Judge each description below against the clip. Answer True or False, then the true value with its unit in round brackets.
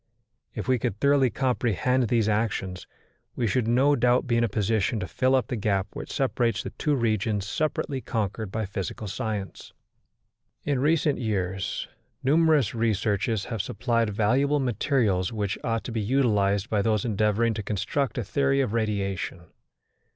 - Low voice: True (115 Hz)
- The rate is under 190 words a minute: True (160 wpm)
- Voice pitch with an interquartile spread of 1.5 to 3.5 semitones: False (3.9 semitones)